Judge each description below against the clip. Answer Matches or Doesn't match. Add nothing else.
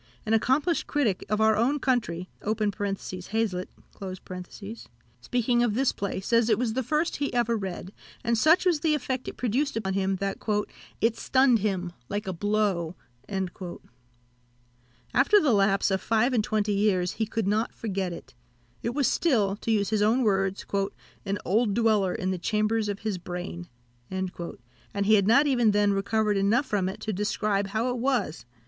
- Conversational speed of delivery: Matches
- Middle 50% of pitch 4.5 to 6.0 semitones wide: Doesn't match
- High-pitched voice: Matches